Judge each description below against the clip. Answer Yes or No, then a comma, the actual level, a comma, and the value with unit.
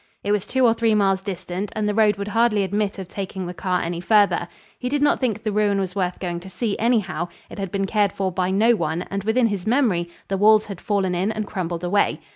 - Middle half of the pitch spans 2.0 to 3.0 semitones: Yes, average, 2.7 semitones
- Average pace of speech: No, fast, 250 wpm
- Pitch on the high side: Yes, high, 200 Hz